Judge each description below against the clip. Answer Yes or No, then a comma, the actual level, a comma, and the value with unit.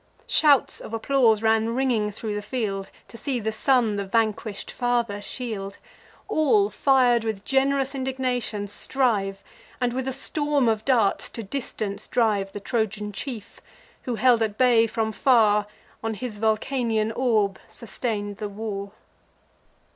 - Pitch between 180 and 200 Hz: No, high, 225 Hz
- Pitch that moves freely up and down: No, average, 3.5 semitones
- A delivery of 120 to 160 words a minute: Yes, average, 140 wpm